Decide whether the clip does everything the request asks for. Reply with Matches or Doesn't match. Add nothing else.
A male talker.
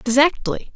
Doesn't match